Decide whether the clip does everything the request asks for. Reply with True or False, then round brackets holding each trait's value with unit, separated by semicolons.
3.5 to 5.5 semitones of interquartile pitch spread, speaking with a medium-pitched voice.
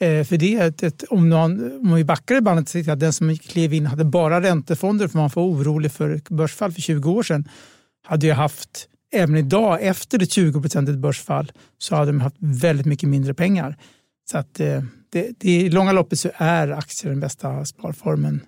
False (3.1 semitones; 160 Hz)